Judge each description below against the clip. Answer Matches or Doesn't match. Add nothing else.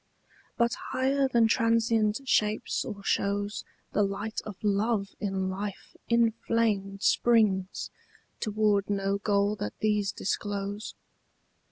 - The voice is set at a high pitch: Matches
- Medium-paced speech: Doesn't match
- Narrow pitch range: Matches